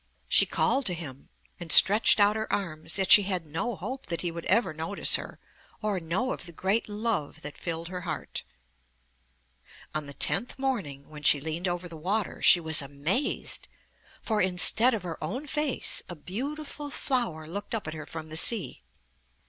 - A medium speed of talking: Yes, average, 180 wpm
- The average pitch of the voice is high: No, medium, 180 Hz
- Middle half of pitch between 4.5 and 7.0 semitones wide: Yes, wide, 5.6 semitones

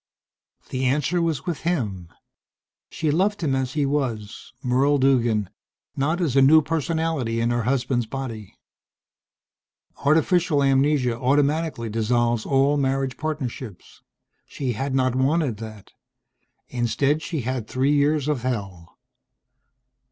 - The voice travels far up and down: No, average, 3.8 semitones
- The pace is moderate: No, slow, 120 wpm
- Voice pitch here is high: No, low, 135 Hz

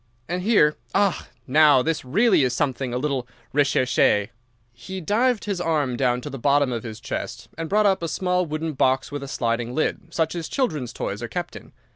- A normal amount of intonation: No, wide, 5.7 semitones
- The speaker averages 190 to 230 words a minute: Yes, average, 195 wpm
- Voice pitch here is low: No, medium, 150 Hz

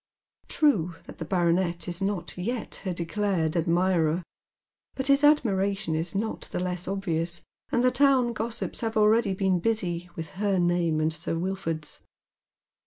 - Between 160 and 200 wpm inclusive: No, average, 150 wpm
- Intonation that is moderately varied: Yes, average, 3.9 semitones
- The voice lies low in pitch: No, medium, 185 Hz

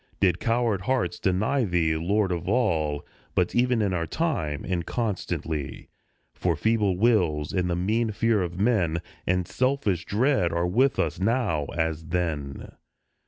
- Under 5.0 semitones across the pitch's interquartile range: No, average, 5.3 semitones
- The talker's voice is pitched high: No, very low, 95 Hz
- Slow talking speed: No, average, 150 wpm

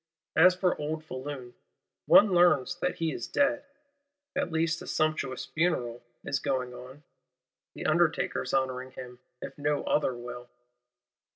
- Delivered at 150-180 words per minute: No, slow, 135 wpm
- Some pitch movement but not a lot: Yes, average, 4.6 semitones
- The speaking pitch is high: No, medium, 145 Hz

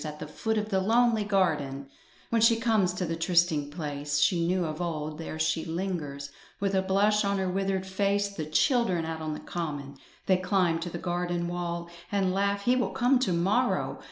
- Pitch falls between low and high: Yes, medium, 180 Hz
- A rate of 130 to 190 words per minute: No, average, 200 wpm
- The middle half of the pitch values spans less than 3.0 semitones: No, average, 3.8 semitones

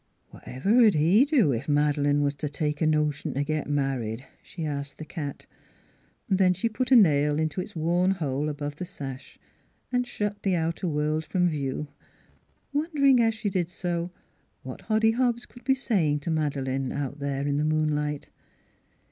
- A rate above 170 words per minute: Yes, average, 180 wpm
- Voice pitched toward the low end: No, medium, 155 Hz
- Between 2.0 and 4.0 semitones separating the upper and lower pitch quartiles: No, average, 5.2 semitones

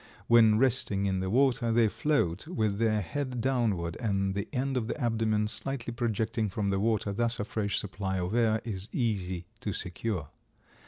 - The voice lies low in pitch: Yes, low, 110 Hz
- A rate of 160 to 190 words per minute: Yes, average, 175 wpm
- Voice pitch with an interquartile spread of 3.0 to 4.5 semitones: Yes, average, 3.3 semitones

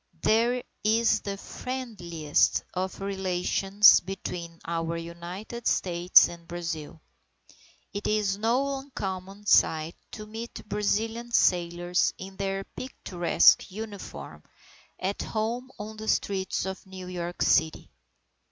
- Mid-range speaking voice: No, high, 195 Hz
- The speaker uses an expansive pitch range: No, average, 3.8 semitones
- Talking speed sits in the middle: No, slow, 110 wpm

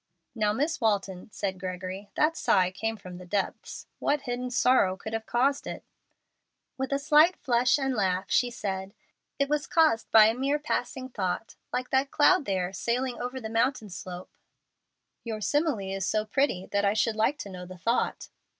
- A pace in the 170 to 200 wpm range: Yes, average, 180 wpm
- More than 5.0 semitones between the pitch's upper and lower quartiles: Yes, wide, 5.6 semitones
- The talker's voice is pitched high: Yes, high, 225 Hz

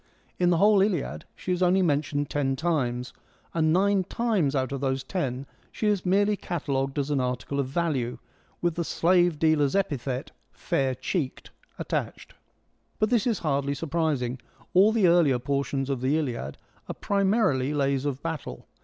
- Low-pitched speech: No, medium, 150 Hz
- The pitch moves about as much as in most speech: Yes, average, 5.0 semitones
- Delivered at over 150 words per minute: Yes, average, 170 wpm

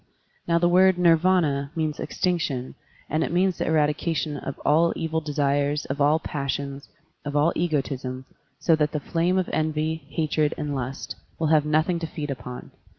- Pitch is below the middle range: No, medium, 155 Hz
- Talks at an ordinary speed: Yes, average, 165 wpm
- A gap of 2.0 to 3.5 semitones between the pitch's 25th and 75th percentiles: Yes, narrow, 2.6 semitones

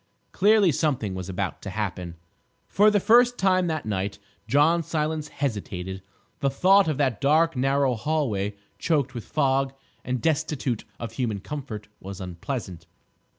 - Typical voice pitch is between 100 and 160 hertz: Yes, low, 135 Hz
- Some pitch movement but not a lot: No, wide, 7.4 semitones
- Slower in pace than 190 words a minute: Yes, average, 150 wpm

